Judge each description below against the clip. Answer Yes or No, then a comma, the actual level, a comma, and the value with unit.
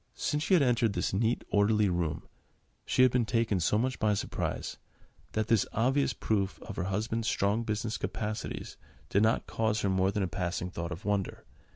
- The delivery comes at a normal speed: Yes, average, 190 wpm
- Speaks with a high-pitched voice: No, low, 105 Hz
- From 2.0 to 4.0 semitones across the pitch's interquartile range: Yes, average, 2.9 semitones